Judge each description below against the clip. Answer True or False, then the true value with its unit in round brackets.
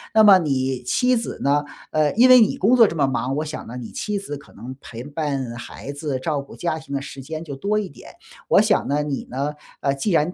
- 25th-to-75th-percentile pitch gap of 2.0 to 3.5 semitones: False (4.8 semitones)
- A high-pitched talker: False (145 Hz)